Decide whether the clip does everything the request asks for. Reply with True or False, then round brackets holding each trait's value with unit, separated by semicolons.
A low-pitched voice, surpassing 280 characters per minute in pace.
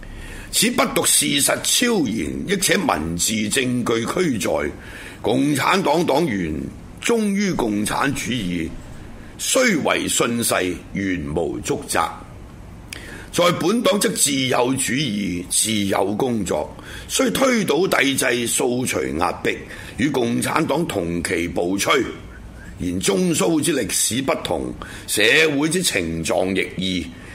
False (105 Hz; 170 characters per minute)